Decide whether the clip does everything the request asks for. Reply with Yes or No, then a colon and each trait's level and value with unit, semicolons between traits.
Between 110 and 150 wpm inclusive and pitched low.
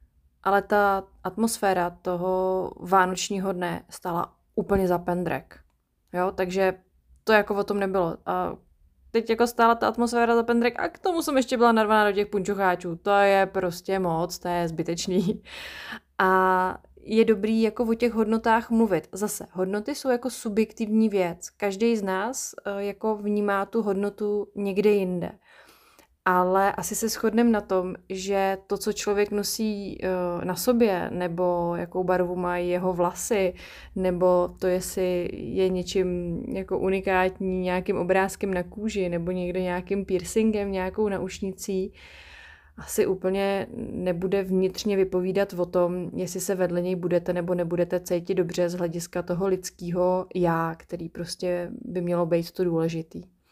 No: average, 145 wpm; high, 190 Hz